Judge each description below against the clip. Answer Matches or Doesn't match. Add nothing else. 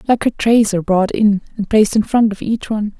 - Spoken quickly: Matches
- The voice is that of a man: Doesn't match